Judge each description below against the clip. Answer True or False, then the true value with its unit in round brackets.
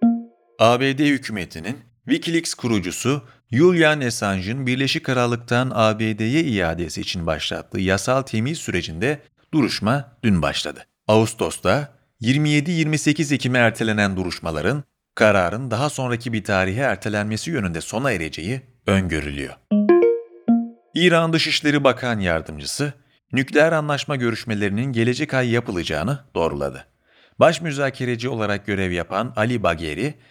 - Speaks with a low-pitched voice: True (120 Hz)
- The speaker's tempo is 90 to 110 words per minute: True (100 wpm)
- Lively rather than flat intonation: True (5.7 semitones)